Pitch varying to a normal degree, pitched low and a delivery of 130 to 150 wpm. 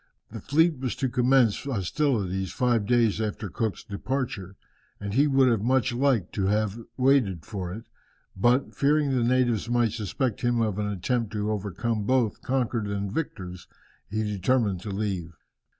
No: average, 4.2 semitones; low, 115 Hz; average, 160 wpm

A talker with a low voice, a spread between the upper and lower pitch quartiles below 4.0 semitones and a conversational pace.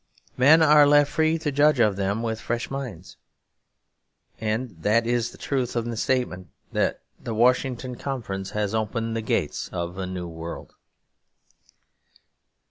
No: low, 115 Hz; average, 4.8 semitones; average, 145 wpm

